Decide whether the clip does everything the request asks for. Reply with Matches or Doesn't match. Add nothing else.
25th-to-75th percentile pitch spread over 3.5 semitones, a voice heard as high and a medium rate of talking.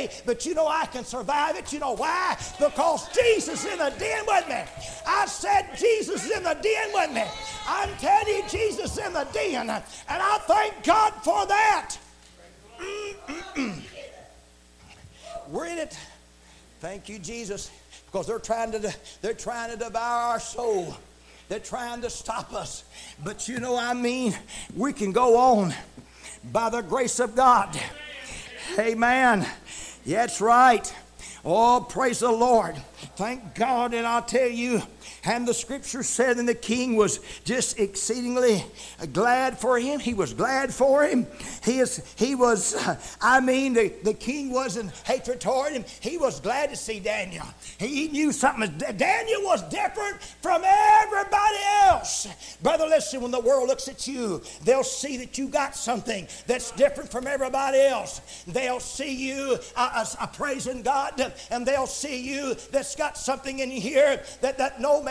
Matches